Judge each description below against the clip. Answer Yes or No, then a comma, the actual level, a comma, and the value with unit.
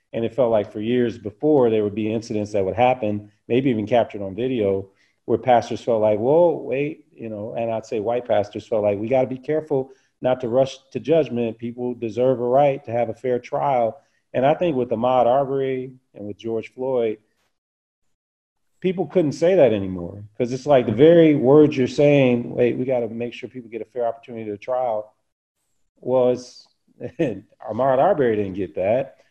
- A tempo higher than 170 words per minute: Yes, average, 190 wpm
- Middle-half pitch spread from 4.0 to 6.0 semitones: No, average, 3.4 semitones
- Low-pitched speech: Yes, low, 120 Hz